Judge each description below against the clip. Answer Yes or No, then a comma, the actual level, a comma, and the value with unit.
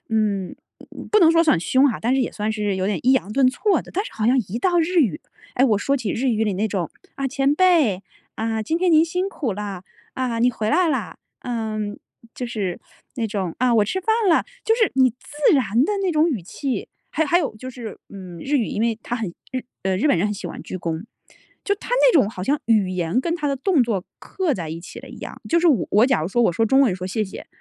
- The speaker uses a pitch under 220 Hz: No, high, 240 Hz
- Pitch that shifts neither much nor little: No, wide, 6.2 semitones